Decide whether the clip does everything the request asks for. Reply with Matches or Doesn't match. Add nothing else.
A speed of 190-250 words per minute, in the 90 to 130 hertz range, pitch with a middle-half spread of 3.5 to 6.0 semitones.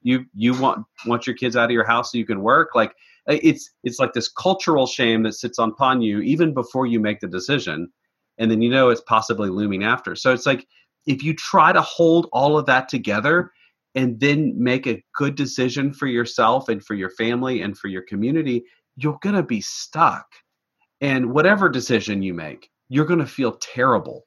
Matches